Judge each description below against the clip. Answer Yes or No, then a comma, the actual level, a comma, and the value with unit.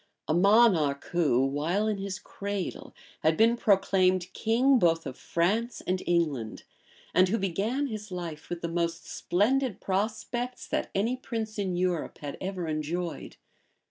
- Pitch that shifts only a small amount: No, average, 4.4 semitones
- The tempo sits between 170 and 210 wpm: No, average, 145 wpm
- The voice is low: No, medium, 185 Hz